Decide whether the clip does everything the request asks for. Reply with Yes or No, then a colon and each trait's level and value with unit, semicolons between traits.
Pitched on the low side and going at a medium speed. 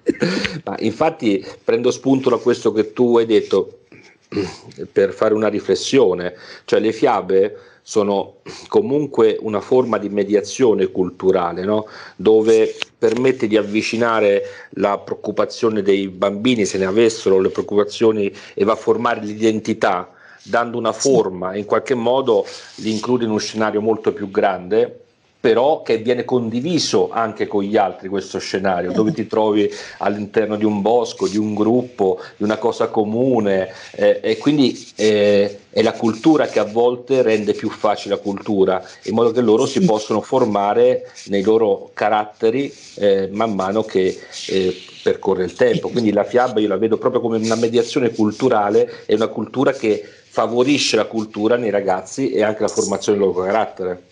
Yes: low, 115 Hz; average, 155 wpm